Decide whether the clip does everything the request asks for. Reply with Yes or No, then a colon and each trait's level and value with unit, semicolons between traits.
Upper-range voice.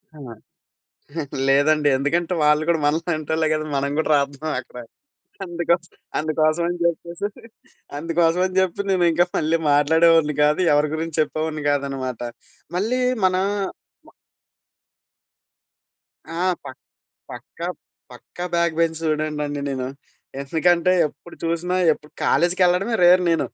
No: medium, 160 Hz